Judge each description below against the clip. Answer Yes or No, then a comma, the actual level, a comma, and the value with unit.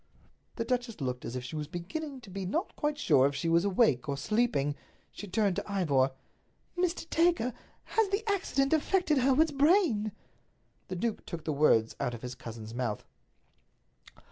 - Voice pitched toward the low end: No, high, 200 Hz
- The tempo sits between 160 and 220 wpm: Yes, average, 170 wpm